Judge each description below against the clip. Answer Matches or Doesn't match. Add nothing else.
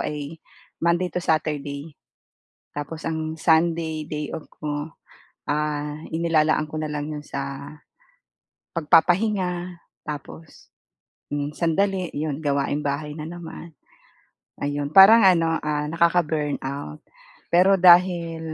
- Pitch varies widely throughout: Doesn't match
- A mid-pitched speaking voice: Matches